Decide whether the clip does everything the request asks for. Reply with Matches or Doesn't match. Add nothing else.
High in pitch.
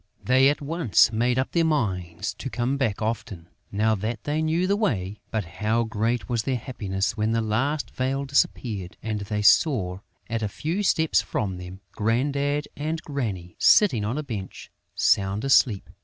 Doesn't match